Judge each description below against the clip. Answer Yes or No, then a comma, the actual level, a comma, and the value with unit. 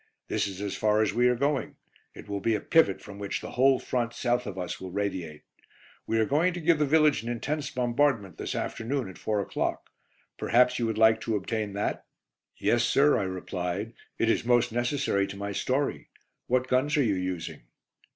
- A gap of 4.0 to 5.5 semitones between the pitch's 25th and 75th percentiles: Yes, average, 4.4 semitones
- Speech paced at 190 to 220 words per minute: Yes, average, 200 wpm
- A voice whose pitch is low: Yes, low, 115 Hz